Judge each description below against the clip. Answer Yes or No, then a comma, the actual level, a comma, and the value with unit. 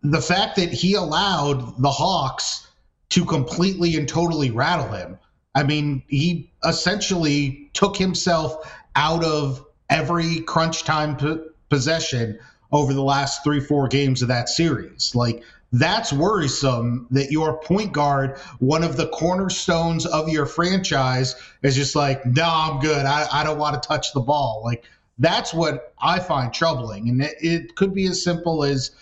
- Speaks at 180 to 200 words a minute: No, average, 155 wpm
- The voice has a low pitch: No, medium, 150 Hz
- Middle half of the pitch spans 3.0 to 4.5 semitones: Yes, average, 3.4 semitones